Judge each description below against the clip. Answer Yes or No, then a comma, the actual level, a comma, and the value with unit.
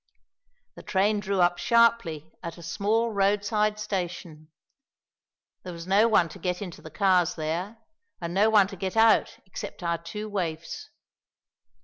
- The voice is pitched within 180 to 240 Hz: Yes, high, 190 Hz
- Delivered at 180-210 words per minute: No, average, 155 wpm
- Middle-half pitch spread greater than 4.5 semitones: No, average, 3.7 semitones